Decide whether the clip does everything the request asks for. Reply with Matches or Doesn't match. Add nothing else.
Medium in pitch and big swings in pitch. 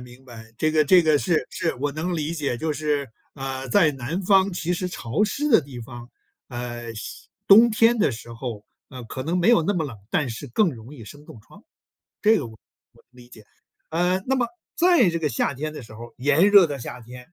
Matches